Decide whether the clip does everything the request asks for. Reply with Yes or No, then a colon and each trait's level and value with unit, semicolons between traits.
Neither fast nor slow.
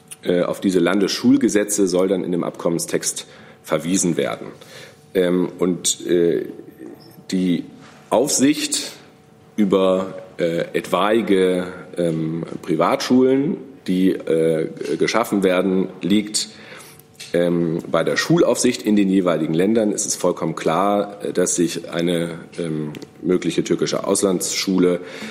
No: slow, 90 wpm